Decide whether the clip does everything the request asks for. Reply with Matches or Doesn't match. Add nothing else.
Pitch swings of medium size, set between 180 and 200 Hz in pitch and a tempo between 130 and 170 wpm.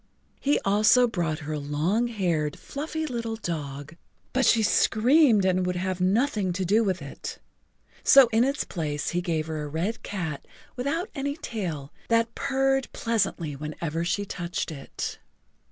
Doesn't match